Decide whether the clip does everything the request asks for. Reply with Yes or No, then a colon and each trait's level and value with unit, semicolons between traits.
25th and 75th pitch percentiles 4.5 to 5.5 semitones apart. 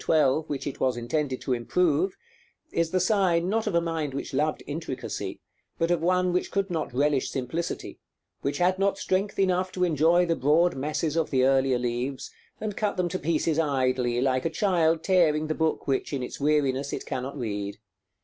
Yes: average, 4.9 semitones